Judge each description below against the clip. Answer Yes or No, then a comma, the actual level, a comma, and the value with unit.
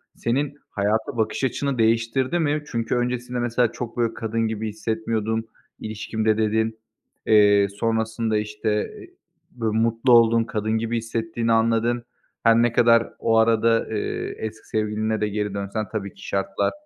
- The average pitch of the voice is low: Yes, low, 115 Hz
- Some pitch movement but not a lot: No, narrow, 1.2 semitones